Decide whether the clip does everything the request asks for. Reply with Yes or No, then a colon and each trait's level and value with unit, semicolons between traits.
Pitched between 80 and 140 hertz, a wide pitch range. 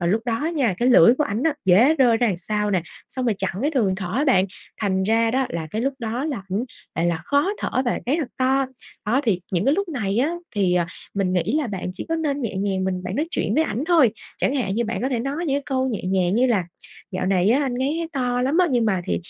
No: high, 235 Hz; wide, 5.9 semitones